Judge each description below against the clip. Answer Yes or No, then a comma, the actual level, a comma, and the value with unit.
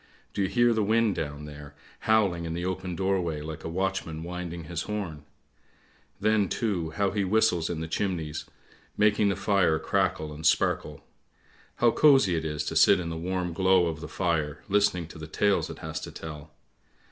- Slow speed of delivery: No, average, 185 wpm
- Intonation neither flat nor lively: Yes, average, 3.9 semitones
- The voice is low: Yes, very low, 90 Hz